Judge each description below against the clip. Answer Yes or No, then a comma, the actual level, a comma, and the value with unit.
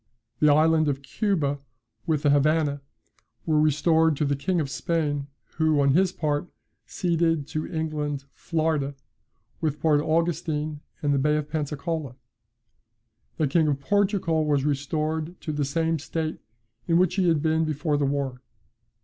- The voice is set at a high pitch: No, medium, 155 Hz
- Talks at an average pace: Yes, average, 150 wpm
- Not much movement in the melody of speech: Yes, narrow, 2.0 semitones